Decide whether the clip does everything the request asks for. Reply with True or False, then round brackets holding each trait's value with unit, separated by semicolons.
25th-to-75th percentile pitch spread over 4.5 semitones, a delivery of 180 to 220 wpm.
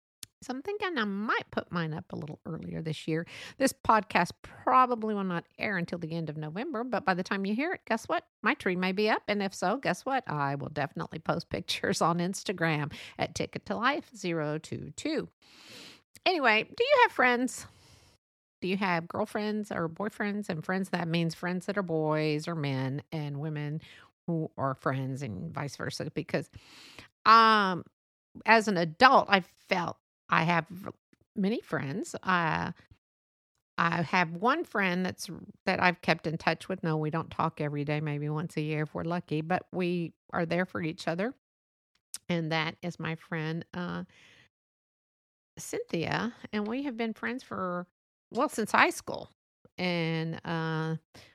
False (4.9 semitones; 170 wpm)